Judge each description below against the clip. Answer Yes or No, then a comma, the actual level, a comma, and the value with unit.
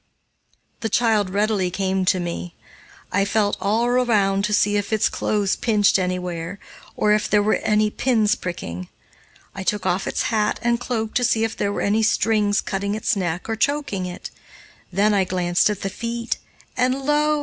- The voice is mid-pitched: No, high, 210 Hz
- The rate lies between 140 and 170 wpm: No, average, 180 wpm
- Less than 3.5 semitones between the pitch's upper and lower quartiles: Yes, average, 2.7 semitones